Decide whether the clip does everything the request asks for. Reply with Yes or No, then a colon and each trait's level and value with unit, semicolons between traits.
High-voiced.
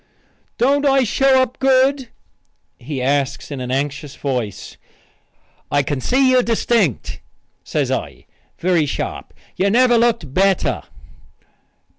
Yes: high, 195 Hz